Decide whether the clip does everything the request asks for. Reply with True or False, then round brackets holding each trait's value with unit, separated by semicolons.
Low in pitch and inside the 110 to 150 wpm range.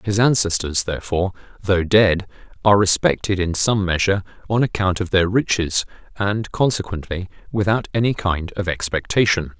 True (95 Hz; 140 wpm)